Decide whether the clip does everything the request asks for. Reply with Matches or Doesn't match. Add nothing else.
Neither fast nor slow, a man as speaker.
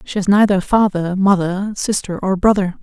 Doesn't match